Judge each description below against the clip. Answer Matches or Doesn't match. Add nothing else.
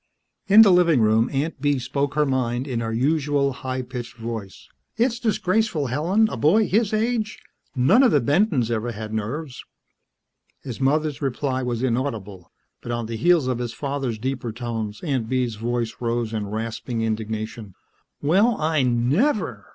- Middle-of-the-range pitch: Doesn't match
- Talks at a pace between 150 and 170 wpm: Matches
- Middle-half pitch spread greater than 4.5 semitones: Matches